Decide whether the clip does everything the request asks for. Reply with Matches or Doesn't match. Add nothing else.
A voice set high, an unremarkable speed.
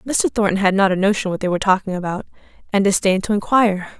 Doesn't match